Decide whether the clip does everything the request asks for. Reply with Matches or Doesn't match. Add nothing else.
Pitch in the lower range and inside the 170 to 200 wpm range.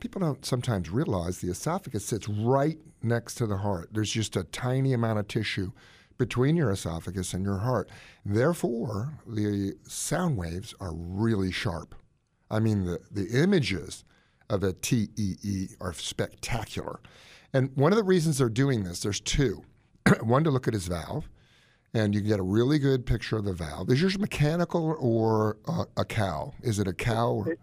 Matches